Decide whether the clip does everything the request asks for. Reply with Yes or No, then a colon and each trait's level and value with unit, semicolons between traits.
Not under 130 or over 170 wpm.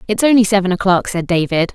No: fast, 205 wpm